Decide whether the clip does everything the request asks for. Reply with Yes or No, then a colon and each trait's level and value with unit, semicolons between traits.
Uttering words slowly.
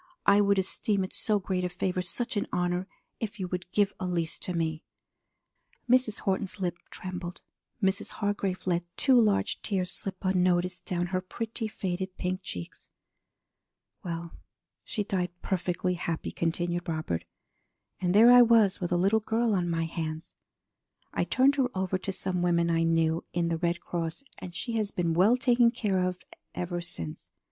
No: average, 170 wpm